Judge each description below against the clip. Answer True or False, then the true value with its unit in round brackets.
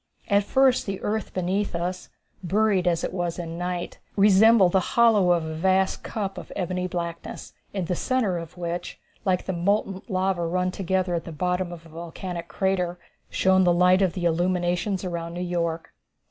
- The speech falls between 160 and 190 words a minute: True (180 wpm)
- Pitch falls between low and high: True (180 Hz)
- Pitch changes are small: True (1.8 semitones)